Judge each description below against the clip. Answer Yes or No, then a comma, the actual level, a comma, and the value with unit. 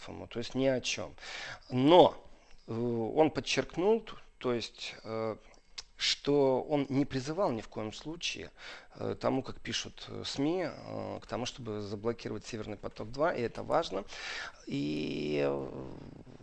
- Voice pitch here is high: No, low, 115 Hz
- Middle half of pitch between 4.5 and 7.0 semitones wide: No, average, 4.1 semitones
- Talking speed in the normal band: Yes, average, 135 wpm